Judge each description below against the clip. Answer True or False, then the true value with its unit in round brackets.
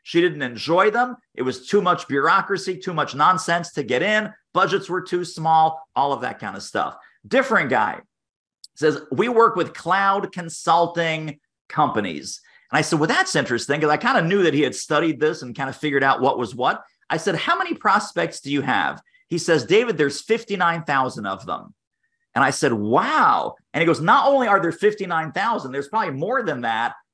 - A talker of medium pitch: True (170 Hz)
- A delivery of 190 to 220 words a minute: True (200 wpm)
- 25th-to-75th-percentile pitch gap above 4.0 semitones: True (5.0 semitones)